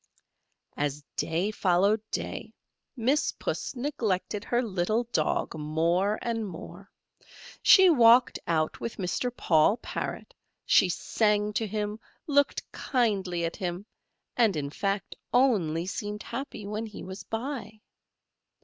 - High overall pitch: Yes, high, 210 Hz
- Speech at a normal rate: No, slow, 120 wpm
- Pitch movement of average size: Yes, average, 4.7 semitones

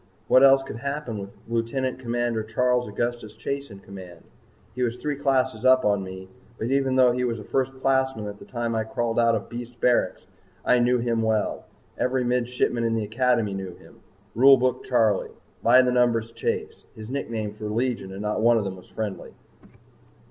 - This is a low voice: Yes, low, 120 Hz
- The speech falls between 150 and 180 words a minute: No, average, 190 wpm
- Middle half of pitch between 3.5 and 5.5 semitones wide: No, average, 2.7 semitones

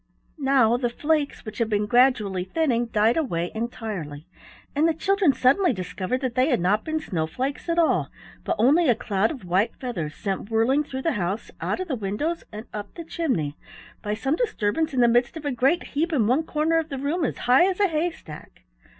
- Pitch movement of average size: No, wide, 6.9 semitones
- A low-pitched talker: No, very high, 250 Hz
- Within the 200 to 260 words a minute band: Yes, fast, 205 wpm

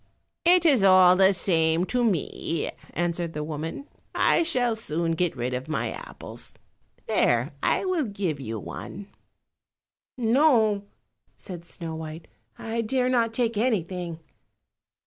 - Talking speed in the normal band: No, slow, 130 wpm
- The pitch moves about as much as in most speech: No, wide, 6.3 semitones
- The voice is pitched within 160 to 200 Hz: Yes, high, 190 Hz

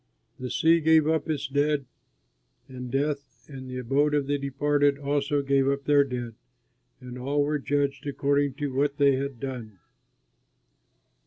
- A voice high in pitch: No, medium, 140 Hz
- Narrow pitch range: Yes, narrow, 1.5 semitones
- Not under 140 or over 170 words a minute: Yes, average, 155 wpm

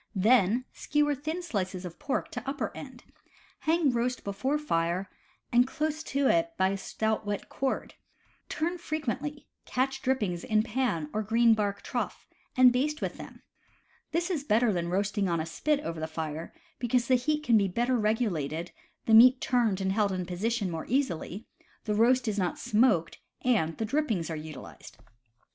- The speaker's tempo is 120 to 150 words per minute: No, average, 175 wpm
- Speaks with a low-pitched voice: No, high, 225 Hz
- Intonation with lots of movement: Yes, wide, 5.9 semitones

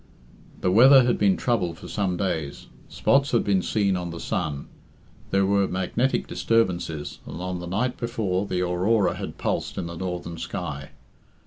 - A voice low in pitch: Yes, very low, 95 Hz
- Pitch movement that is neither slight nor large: Yes, average, 3.9 semitones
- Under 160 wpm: No, average, 165 wpm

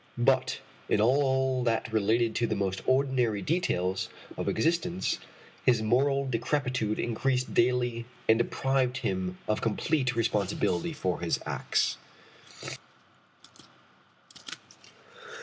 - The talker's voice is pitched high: No, low, 120 Hz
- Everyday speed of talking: No, slow, 100 wpm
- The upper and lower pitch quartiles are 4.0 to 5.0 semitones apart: No, average, 3.6 semitones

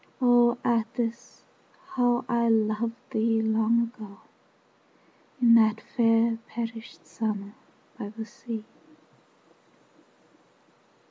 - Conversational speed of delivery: No, slow, 85 wpm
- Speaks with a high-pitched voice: Yes, high, 230 Hz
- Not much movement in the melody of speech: Yes, narrow, 1.3 semitones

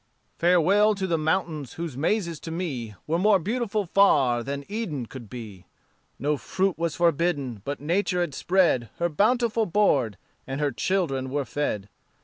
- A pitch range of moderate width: No, wide, 5.9 semitones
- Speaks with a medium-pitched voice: Yes, medium, 165 Hz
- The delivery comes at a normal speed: Yes, average, 155 wpm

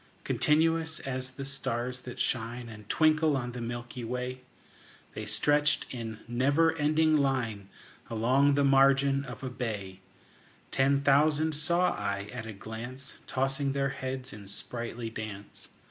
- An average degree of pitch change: Yes, average, 3.4 semitones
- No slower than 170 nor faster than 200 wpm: No, average, 140 wpm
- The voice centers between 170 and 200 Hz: No, low, 130 Hz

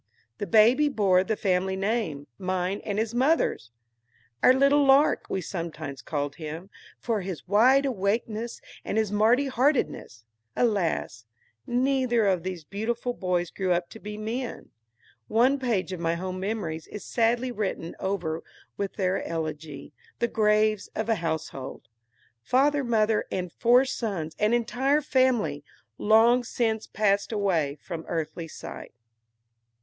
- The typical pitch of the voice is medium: No, high, 210 Hz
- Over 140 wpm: No, slow, 135 wpm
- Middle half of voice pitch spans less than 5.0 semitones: No, wide, 5.5 semitones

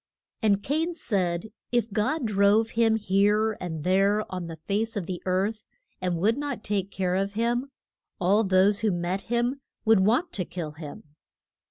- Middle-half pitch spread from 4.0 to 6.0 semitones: No, average, 3.3 semitones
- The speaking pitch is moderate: No, high, 205 Hz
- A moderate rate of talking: Yes, average, 175 wpm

